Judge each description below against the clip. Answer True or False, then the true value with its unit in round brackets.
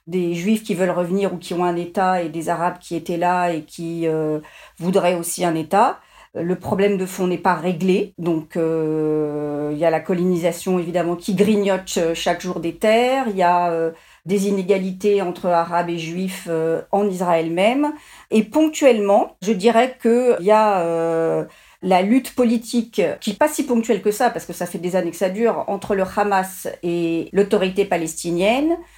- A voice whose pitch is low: False (185 Hz)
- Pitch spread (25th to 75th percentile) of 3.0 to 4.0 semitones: True (3.3 semitones)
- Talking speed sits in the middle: True (190 wpm)